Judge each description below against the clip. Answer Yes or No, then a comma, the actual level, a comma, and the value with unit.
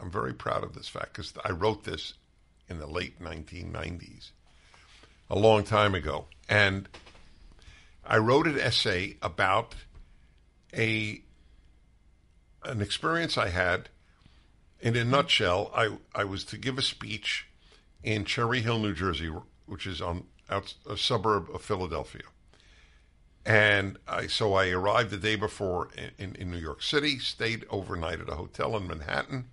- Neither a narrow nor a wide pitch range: Yes, average, 4.7 semitones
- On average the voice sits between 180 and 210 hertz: No, very low, 95 Hz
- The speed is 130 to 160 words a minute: Yes, average, 150 wpm